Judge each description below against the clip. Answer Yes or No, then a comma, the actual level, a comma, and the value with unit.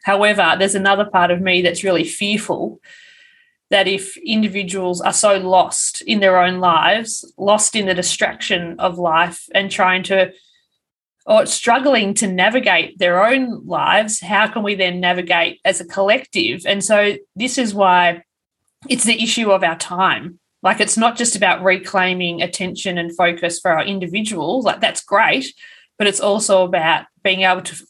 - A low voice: No, high, 195 Hz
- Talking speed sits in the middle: Yes, average, 165 wpm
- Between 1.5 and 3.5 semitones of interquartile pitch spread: Yes, average, 3.0 semitones